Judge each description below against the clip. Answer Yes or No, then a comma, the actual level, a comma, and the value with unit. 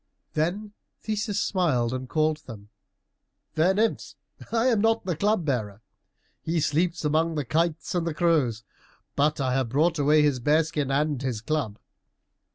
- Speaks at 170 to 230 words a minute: No, average, 155 wpm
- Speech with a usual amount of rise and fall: Yes, average, 4.5 semitones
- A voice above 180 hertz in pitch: No, medium, 155 Hz